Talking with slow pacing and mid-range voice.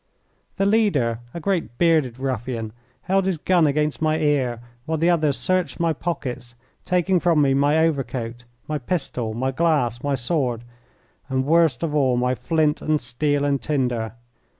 No: average, 160 wpm; medium, 145 Hz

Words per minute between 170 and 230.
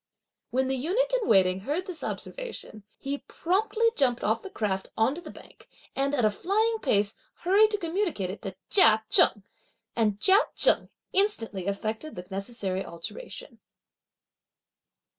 No: average, 155 wpm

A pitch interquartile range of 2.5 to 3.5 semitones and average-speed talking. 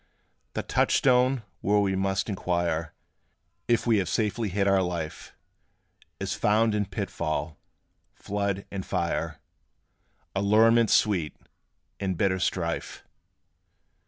No: average, 2.9 semitones; slow, 105 wpm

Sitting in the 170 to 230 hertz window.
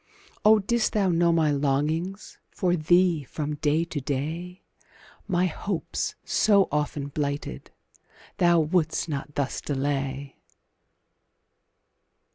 No: medium, 155 Hz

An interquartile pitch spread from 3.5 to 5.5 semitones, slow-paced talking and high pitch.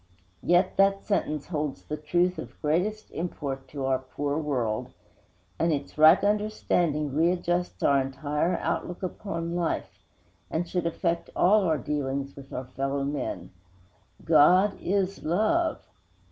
No: average, 4.3 semitones; slow, 130 wpm; medium, 160 Hz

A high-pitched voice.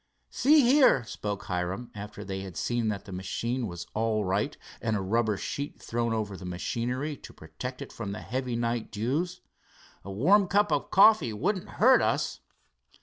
No: low, 115 Hz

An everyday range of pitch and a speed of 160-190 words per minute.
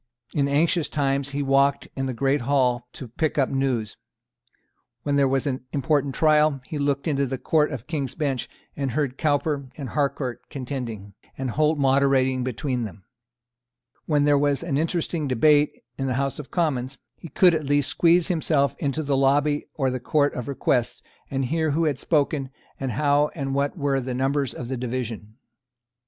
No: narrow, 2.2 semitones; average, 180 wpm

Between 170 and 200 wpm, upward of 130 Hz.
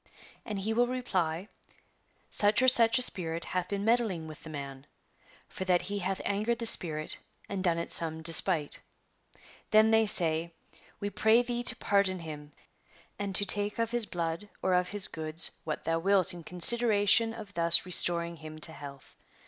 Yes: average, 180 wpm; medium, 185 Hz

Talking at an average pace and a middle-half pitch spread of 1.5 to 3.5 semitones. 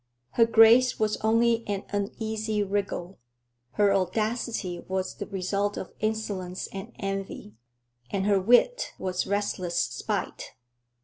No: slow, 120 wpm; narrow, 2.5 semitones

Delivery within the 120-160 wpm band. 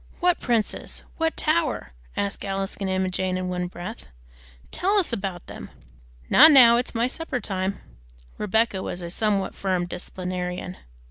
Yes: average, 150 wpm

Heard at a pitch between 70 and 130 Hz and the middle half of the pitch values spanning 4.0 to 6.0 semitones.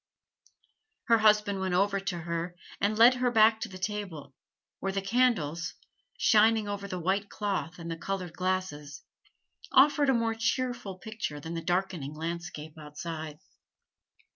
No: high, 190 Hz; average, 4.5 semitones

